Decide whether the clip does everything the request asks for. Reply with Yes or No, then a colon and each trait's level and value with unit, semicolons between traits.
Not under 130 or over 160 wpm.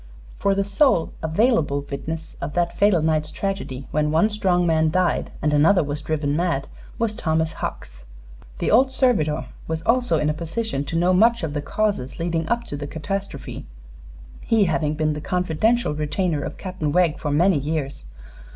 No: average, 175 wpm